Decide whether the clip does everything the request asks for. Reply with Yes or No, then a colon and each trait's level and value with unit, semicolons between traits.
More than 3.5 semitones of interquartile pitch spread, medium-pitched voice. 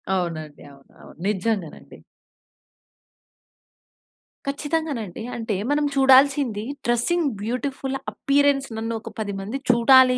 No: average, 4.8 semitones; high, 245 Hz